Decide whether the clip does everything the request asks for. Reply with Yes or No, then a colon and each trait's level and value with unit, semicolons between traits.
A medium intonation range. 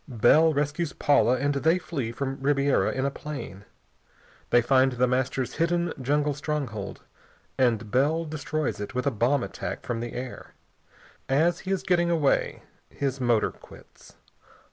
Yes: average, 3.4 semitones